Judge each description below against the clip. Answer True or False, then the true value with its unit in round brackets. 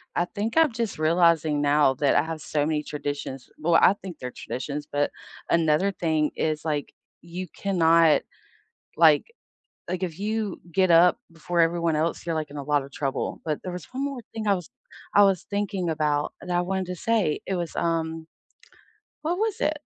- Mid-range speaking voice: True (170 Hz)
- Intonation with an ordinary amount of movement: True (4.0 semitones)